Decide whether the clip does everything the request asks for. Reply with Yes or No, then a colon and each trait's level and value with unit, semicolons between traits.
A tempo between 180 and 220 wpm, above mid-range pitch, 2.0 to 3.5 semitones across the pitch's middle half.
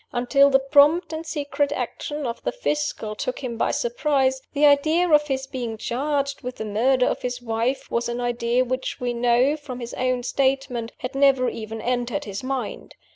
Yes: average, 185 wpm; very high, 255 Hz; average, 2.8 semitones